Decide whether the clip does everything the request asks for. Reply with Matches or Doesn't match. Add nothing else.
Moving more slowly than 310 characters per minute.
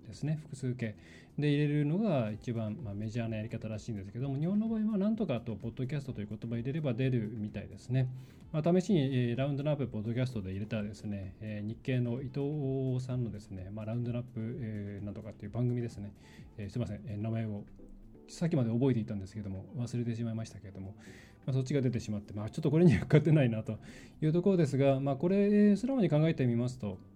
Doesn't match